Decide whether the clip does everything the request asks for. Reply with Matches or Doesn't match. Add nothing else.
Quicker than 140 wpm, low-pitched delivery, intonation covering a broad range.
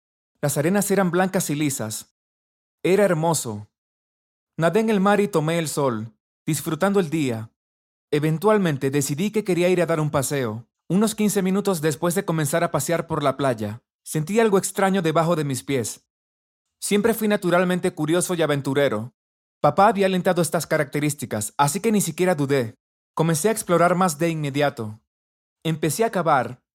Doesn't match